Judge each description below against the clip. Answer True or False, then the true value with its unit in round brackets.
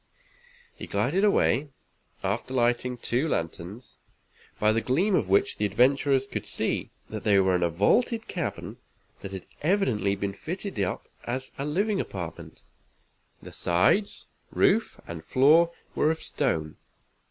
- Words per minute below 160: True (140 wpm)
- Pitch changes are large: True (8.6 semitones)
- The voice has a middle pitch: False (125 Hz)